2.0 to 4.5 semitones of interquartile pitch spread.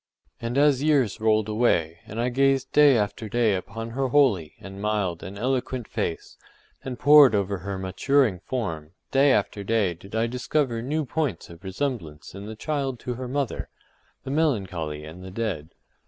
No: wide, 5.5 semitones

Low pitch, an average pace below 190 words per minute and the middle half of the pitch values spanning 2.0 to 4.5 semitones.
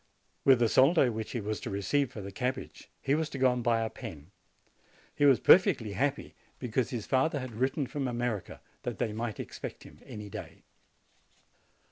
No: low, 125 Hz; average, 200 wpm; average, 3.7 semitones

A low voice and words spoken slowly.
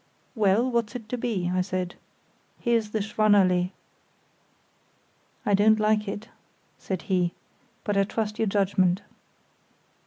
No: high, 205 Hz; slow, 125 wpm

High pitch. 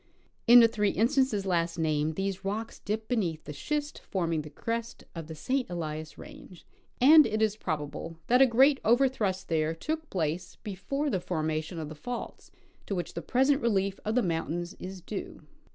Yes: high, 195 Hz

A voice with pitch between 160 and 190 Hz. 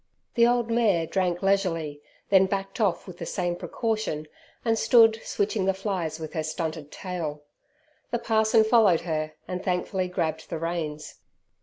Yes: medium, 185 Hz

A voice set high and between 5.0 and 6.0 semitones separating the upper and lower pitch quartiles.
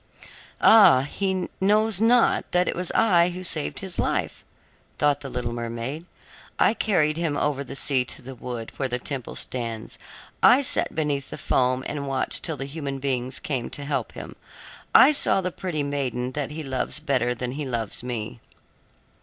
No: medium, 140 Hz; wide, 5.4 semitones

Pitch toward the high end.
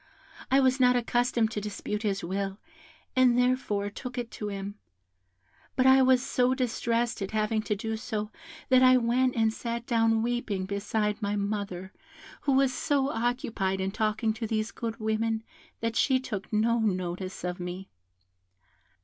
Yes: high, 225 Hz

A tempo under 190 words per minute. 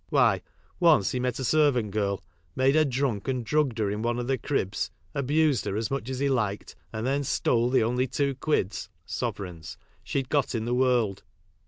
No: average, 195 wpm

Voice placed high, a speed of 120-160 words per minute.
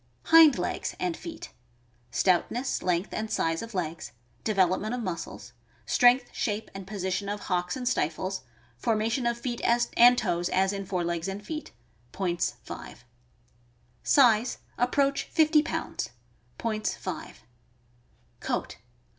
Yes: high, 210 Hz; slow, 135 wpm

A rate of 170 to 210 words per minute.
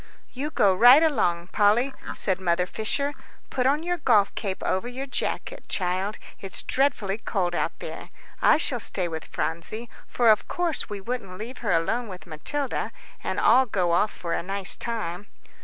Yes: average, 175 wpm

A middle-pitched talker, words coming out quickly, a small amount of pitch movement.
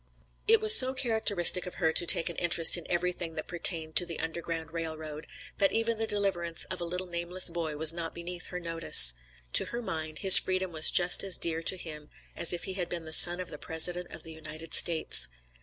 Yes: medium, 170 Hz; fast, 225 wpm; narrow, 2.0 semitones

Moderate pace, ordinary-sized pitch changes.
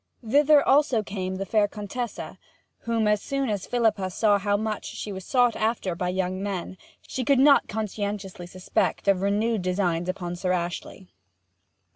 Yes: average, 160 wpm; average, 3.4 semitones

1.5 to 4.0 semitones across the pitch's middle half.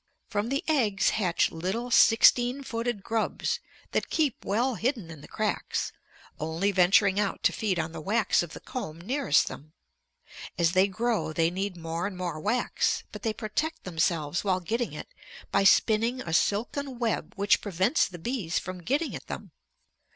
No: wide, 5.4 semitones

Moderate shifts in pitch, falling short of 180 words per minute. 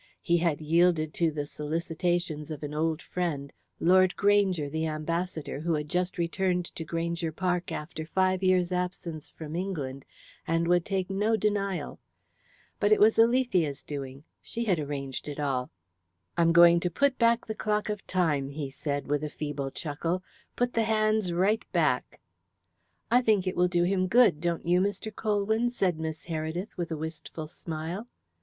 Yes: average, 3.7 semitones; average, 170 wpm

